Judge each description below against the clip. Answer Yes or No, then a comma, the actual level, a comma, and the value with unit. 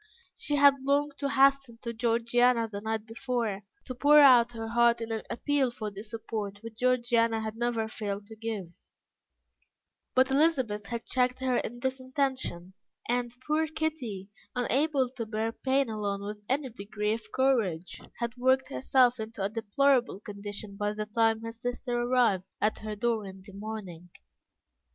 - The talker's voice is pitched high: Yes, high, 230 Hz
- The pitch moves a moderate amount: Yes, average, 3.4 semitones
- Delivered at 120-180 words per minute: Yes, average, 165 wpm